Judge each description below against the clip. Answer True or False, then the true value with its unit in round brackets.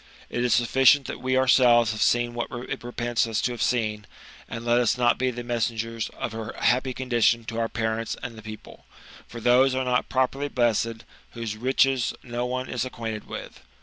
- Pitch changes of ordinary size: False (1.7 semitones)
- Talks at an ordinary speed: True (195 wpm)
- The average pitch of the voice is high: False (120 Hz)